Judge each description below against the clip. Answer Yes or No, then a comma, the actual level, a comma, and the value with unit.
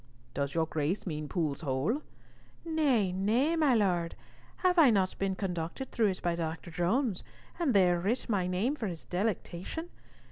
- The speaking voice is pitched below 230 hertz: Yes, high, 190 Hz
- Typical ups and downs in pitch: No, wide, 6.1 semitones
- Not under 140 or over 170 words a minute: Yes, average, 165 wpm